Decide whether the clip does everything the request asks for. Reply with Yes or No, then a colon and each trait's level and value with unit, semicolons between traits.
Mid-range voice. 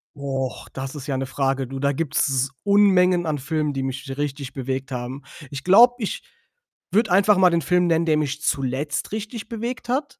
Yes: medium, 150 Hz